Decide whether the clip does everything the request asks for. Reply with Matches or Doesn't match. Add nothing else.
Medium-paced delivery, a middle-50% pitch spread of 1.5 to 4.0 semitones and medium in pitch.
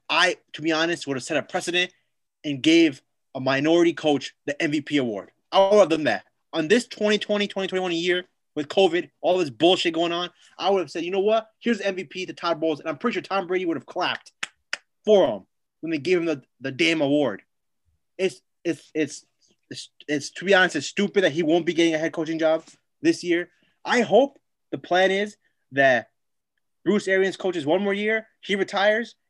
Doesn't match